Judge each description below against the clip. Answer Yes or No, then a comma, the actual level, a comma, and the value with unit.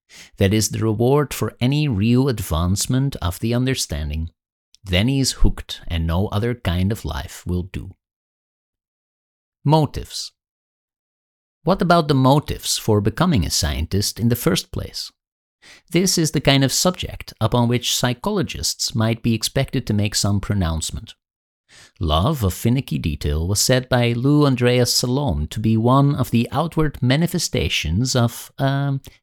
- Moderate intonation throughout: No, wide, 6.9 semitones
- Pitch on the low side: Yes, low, 110 Hz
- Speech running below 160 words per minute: Yes, average, 150 wpm